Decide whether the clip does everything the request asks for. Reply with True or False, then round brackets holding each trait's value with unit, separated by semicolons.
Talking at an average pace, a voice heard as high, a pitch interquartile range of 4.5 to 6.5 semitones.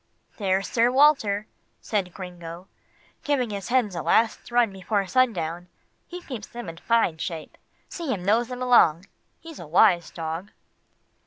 True (150 wpm; 205 Hz; 5.5 semitones)